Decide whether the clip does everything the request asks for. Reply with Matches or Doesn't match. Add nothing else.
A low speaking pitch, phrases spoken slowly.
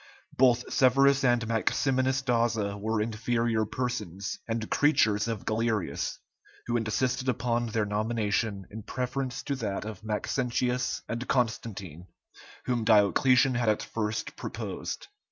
Matches